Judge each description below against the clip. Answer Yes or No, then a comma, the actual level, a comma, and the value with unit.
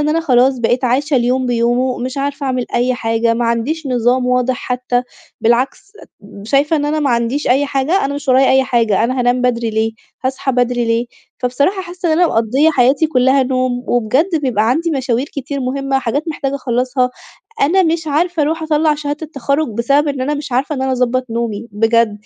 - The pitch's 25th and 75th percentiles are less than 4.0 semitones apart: Yes, average, 3.0 semitones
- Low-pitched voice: No, very high, 260 Hz